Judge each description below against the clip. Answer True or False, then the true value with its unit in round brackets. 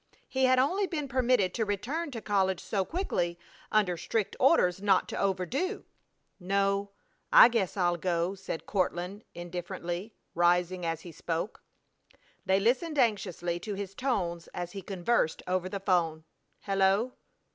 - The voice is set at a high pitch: True (195 Hz)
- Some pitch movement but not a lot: True (4.4 semitones)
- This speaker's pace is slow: False (145 wpm)